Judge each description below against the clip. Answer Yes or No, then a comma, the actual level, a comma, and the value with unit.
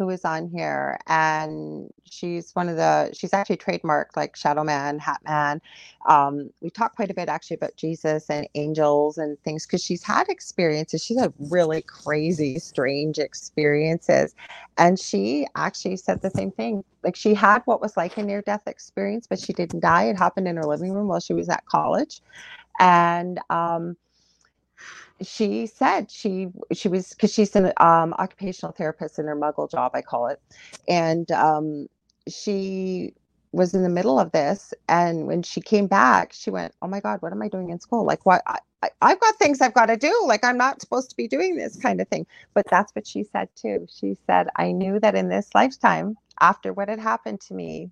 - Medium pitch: Yes, medium, 180 Hz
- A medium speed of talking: Yes, average, 195 wpm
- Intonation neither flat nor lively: Yes, average, 4.7 semitones